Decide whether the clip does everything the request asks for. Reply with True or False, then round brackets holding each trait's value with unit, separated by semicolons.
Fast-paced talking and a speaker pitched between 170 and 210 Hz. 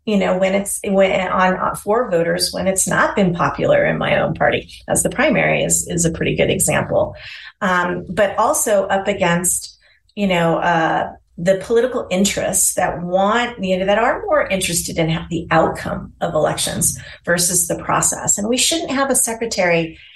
False (180 wpm; 190 Hz)